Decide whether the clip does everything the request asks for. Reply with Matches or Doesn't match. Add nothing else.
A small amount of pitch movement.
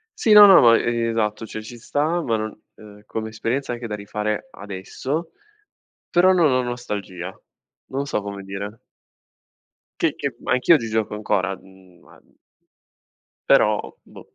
Doesn't match